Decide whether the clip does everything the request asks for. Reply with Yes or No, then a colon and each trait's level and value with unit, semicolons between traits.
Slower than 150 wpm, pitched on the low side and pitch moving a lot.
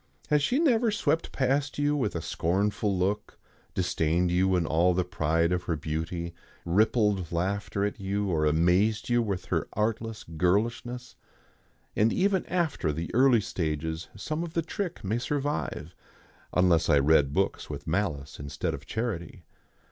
No: average, 155 wpm; very low, 95 Hz; wide, 6.2 semitones